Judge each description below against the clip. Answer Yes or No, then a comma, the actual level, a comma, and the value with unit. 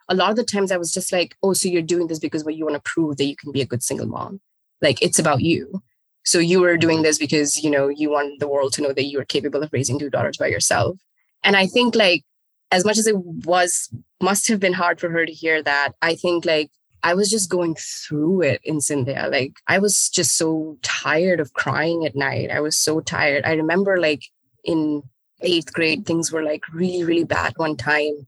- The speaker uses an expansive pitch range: No, average, 3.6 semitones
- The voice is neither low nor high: Yes, medium, 160 Hz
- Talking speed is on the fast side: Yes, fast, 240 wpm